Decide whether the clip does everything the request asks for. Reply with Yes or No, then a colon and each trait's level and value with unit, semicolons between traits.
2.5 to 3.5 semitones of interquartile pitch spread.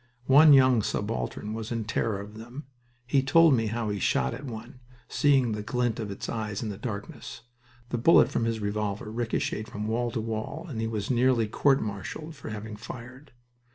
Yes: average, 3.0 semitones